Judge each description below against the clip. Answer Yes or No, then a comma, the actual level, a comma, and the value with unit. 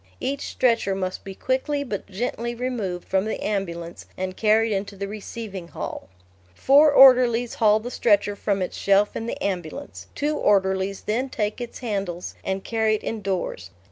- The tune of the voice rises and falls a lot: No, average, 3.8 semitones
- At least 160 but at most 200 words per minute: Yes, average, 165 wpm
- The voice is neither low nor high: No, high, 210 Hz